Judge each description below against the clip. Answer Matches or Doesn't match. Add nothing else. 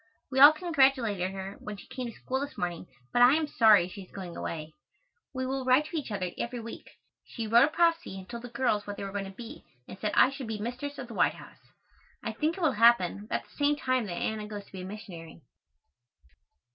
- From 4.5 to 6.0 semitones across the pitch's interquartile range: Matches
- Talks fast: Matches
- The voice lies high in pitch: Matches